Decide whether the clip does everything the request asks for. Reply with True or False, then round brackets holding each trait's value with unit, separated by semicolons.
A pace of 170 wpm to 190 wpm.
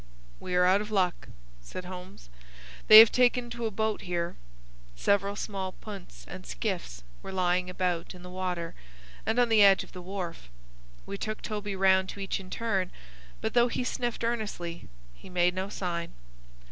True (175 wpm)